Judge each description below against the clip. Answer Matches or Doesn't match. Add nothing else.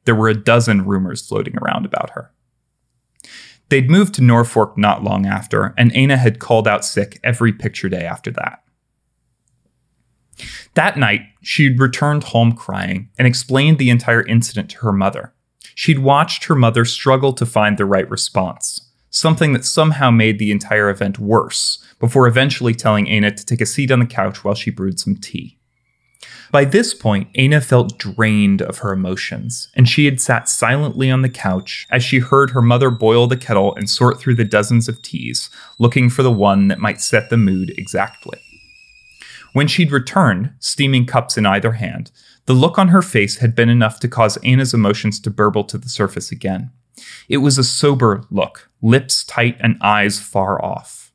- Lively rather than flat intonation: Doesn't match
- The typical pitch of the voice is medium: Doesn't match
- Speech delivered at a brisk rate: Doesn't match